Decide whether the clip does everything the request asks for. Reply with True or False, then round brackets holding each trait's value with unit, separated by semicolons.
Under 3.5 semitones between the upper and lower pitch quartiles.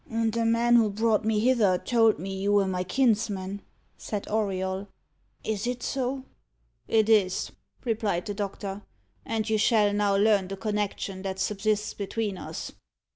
True (2.4 semitones)